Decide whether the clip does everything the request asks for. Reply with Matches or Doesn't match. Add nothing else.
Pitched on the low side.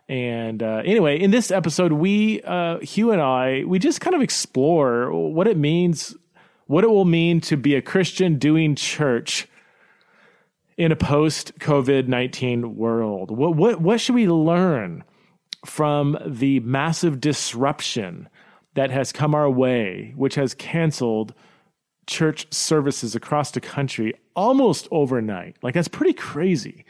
Doesn't match